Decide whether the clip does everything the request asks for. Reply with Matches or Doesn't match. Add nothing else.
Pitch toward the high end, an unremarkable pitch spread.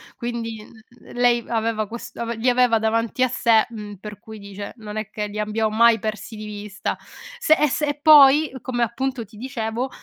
Doesn't match